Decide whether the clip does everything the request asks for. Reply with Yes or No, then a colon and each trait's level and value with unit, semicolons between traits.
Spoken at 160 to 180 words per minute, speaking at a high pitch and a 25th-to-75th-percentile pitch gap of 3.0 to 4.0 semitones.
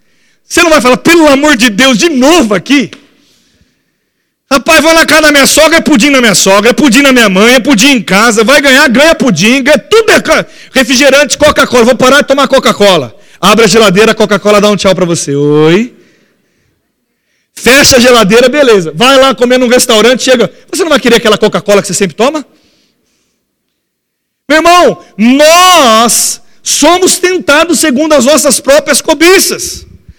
No: average, 170 wpm; very high, 265 Hz; average, 5.2 semitones